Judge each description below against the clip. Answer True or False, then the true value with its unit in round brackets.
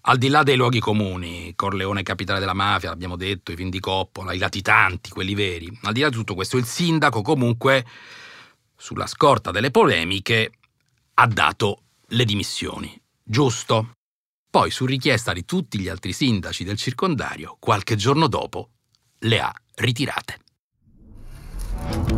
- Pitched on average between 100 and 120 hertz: True (105 Hz)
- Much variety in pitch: False (4.6 semitones)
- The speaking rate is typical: True (140 wpm)